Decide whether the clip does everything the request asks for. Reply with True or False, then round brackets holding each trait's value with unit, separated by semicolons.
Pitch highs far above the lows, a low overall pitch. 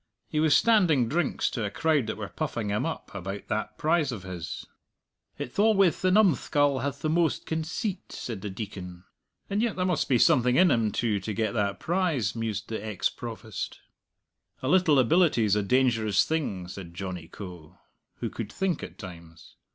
True (7.9 semitones; 120 Hz)